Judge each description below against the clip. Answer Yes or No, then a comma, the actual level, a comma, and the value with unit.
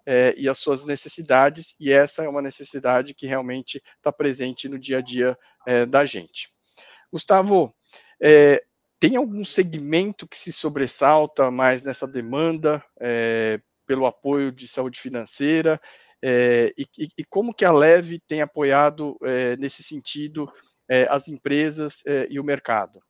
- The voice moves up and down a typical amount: Yes, average, 3.2 semitones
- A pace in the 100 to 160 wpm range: Yes, average, 150 wpm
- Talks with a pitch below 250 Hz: Yes, medium, 140 Hz